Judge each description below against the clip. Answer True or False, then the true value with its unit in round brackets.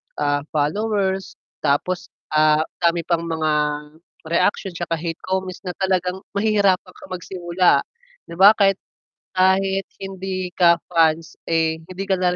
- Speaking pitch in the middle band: True (180 Hz)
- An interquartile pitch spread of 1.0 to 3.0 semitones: True (2.5 semitones)